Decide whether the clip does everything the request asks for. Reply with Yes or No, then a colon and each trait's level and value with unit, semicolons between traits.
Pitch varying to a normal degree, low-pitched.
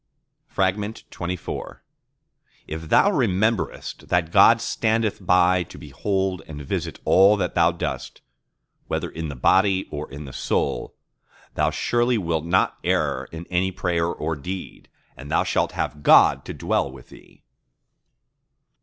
Yes: average, 3.4 semitones; very low, 90 Hz